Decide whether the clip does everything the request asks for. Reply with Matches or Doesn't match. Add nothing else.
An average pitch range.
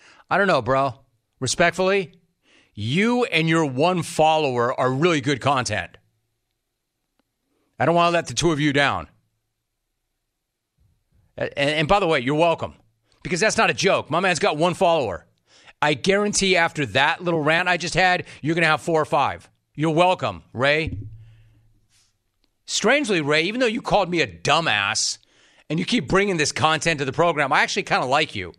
Doesn't match